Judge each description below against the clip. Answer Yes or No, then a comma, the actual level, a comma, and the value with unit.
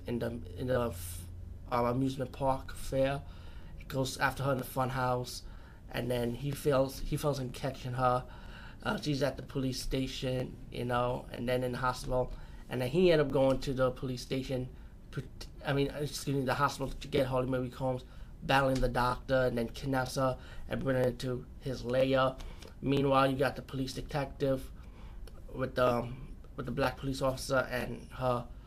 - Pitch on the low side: Yes, low, 130 Hz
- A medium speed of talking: Yes, average, 180 wpm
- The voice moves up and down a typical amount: No, narrow, 1.6 semitones